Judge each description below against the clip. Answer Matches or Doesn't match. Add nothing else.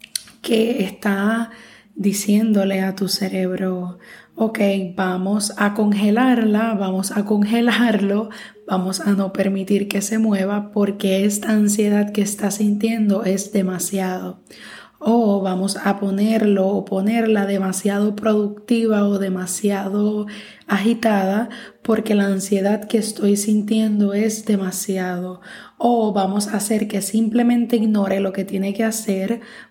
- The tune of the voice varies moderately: Doesn't match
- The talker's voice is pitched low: Doesn't match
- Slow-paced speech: Matches